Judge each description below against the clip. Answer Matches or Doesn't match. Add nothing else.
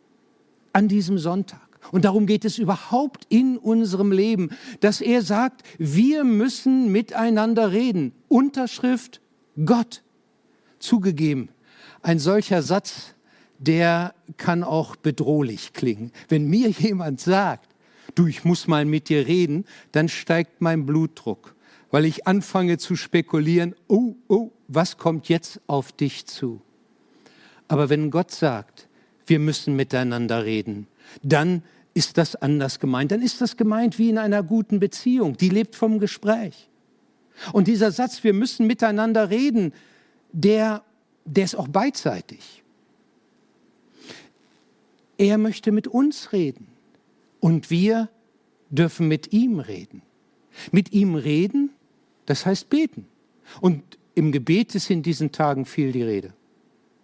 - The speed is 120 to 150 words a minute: Matches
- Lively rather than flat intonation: Matches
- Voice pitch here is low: Doesn't match